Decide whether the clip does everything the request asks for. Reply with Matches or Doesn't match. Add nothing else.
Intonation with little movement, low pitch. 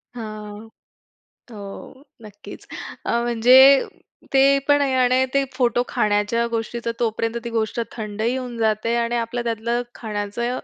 Doesn't match